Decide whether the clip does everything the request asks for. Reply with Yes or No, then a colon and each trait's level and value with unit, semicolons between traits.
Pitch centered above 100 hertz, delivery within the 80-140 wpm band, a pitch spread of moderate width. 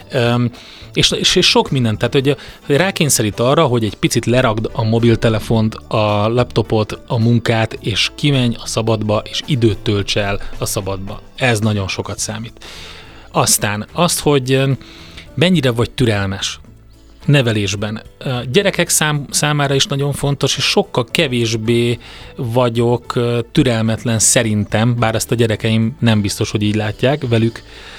Yes: low, 115 Hz; average, 135 wpm; average, 3.7 semitones